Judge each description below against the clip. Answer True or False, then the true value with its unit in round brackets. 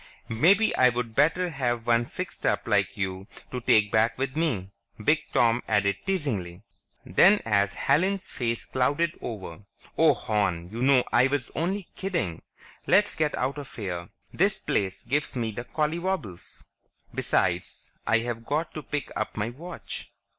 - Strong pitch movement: True (6.5 semitones)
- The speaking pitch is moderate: False (120 Hz)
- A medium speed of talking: True (150 wpm)